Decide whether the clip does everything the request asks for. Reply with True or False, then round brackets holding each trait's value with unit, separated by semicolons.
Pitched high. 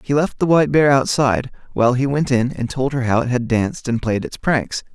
False (130 Hz)